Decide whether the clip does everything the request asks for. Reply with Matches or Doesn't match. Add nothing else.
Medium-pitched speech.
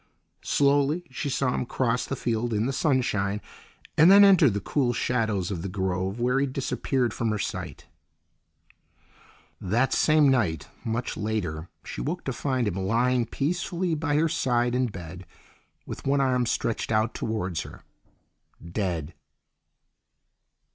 Doesn't match